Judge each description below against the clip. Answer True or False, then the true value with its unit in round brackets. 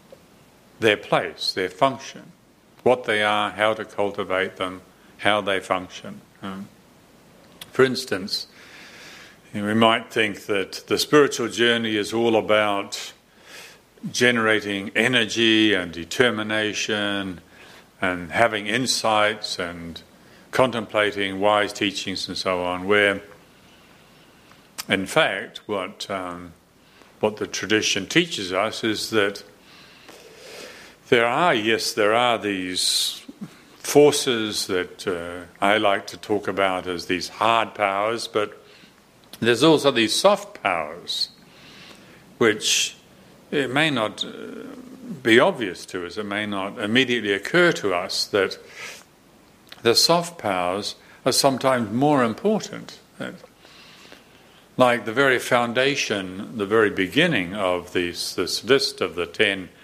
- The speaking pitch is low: True (110 Hz)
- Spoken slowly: True (115 wpm)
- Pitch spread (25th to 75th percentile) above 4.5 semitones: True (5.0 semitones)